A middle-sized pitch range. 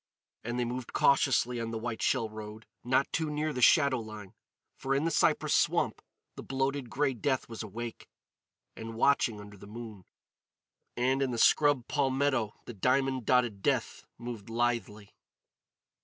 Yes: average, 3.3 semitones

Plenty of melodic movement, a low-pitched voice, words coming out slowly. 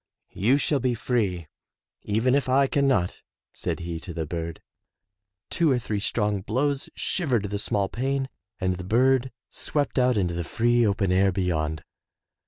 No: wide, 6.1 semitones; low, 110 Hz; average, 165 wpm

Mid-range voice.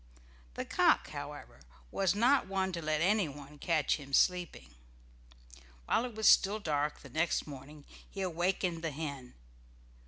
Yes: medium, 165 Hz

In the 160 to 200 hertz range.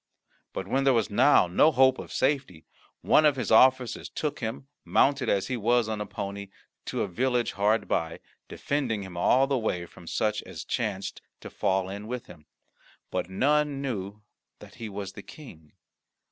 No: low, 110 Hz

